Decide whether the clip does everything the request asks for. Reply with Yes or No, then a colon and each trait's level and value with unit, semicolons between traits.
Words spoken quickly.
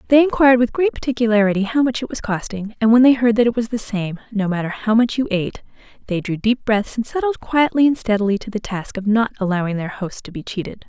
Yes: fast, 250 wpm